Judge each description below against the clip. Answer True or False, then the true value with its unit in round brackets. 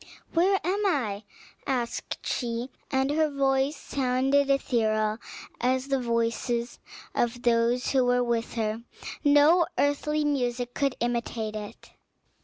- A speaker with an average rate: False (120 wpm)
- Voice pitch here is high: True (255 Hz)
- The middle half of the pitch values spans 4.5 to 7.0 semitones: False (3.3 semitones)